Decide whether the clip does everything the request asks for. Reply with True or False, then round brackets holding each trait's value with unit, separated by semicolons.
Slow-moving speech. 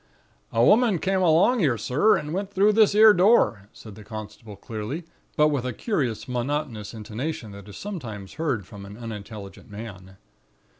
False (165 wpm)